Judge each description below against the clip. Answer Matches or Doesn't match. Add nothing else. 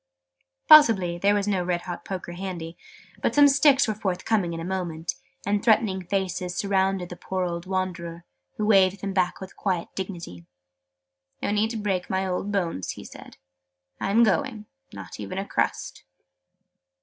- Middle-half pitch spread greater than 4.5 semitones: Doesn't match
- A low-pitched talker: Doesn't match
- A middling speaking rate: Matches